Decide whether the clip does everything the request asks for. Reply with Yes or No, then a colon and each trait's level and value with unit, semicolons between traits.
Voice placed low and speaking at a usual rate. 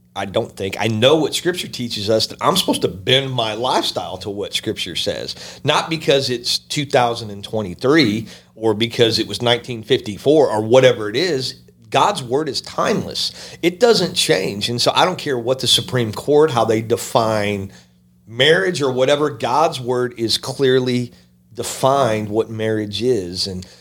Yes: low, 115 Hz; average, 170 wpm